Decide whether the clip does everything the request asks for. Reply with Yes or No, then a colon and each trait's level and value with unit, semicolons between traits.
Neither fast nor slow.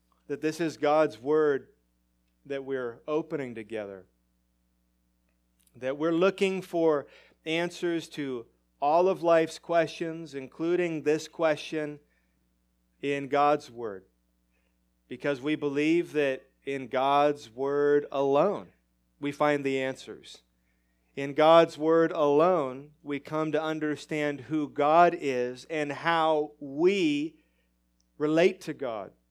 No: slow, 110 wpm